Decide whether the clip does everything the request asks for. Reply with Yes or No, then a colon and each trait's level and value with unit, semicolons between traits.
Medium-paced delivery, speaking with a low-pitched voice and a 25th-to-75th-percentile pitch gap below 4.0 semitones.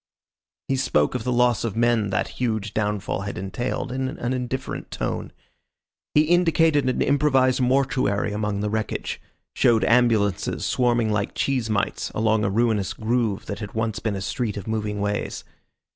Yes: average, 160 wpm; low, 115 Hz; average, 3.5 semitones